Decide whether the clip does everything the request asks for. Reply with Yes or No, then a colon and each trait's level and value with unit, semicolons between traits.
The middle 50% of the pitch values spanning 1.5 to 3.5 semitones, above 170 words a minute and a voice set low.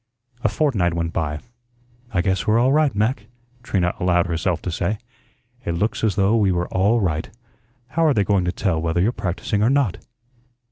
No: average, 4.1 semitones; average, 190 wpm; very low, 95 Hz